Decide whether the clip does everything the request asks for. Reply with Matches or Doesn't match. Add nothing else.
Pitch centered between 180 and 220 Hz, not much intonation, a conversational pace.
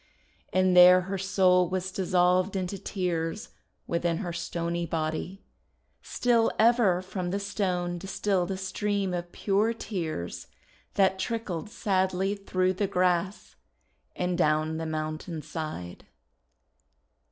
Doesn't match